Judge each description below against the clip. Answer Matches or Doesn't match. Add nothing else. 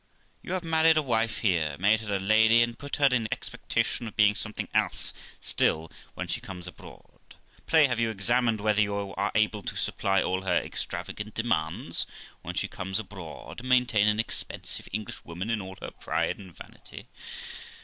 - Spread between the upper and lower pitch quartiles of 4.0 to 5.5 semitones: Doesn't match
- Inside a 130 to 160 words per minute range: Doesn't match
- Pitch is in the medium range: Doesn't match